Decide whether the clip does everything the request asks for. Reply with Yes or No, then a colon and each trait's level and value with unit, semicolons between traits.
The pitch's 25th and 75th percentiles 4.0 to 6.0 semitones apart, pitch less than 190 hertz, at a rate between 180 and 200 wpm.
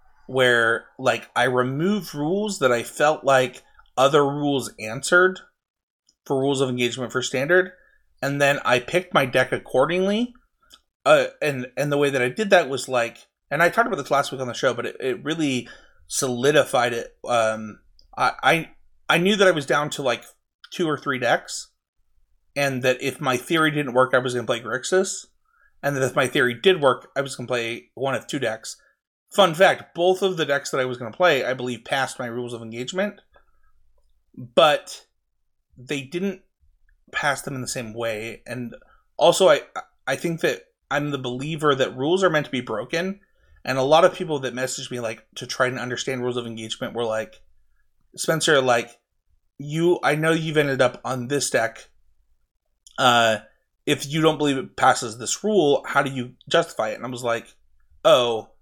Yes: average, 5.0 semitones; low, 135 Hz; average, 190 wpm